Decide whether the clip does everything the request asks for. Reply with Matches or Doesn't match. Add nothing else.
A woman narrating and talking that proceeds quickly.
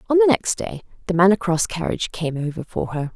Matches